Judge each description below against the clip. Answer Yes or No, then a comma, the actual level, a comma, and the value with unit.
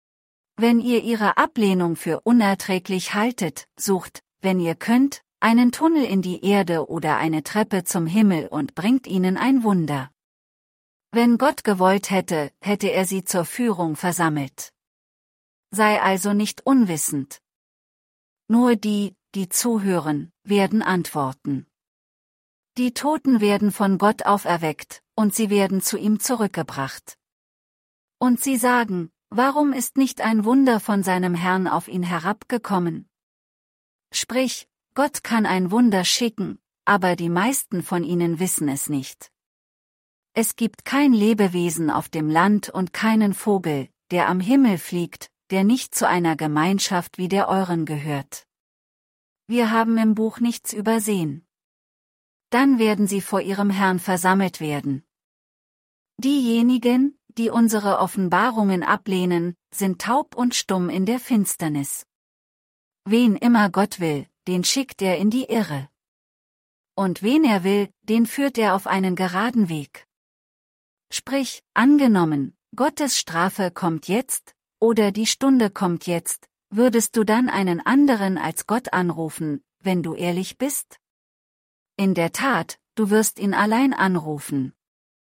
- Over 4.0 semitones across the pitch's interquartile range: Yes, average, 4.9 semitones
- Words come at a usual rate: No, slow, 130 wpm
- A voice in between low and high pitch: No, high, 195 Hz